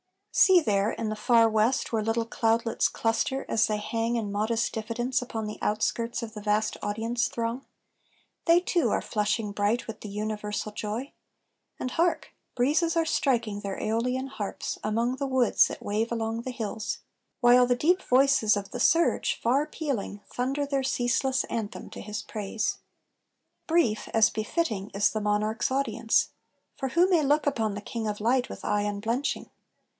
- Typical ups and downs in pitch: Yes, average, 3.4 semitones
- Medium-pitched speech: No, high, 230 Hz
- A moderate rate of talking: Yes, average, 170 wpm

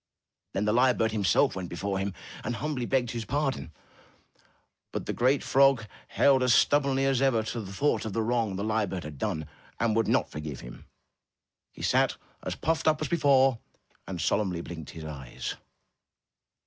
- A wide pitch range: Yes, wide, 5.9 semitones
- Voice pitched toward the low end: Yes, low, 115 Hz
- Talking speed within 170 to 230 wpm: Yes, average, 180 wpm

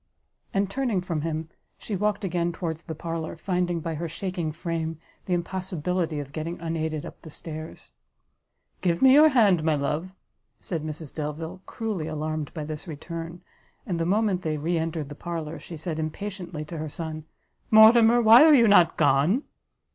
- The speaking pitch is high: No, medium, 165 Hz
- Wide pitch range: No, average, 3.1 semitones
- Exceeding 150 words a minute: Yes, average, 170 wpm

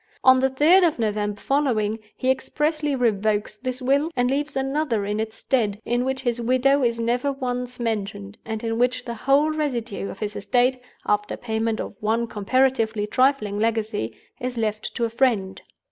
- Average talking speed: Yes, average, 175 wpm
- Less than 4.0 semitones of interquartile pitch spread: Yes, average, 3.5 semitones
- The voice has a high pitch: Yes, high, 240 Hz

